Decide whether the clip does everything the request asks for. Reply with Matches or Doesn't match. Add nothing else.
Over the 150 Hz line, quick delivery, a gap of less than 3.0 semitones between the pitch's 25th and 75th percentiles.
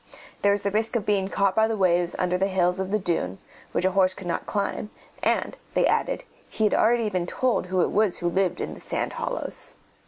Matches